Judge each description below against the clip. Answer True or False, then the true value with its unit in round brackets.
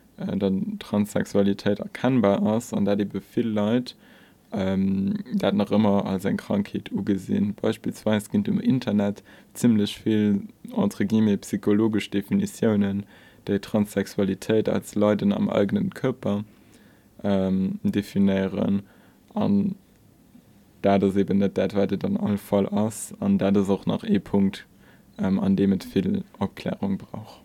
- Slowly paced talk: True (125 wpm)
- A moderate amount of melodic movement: True (4.1 semitones)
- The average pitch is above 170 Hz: False (105 Hz)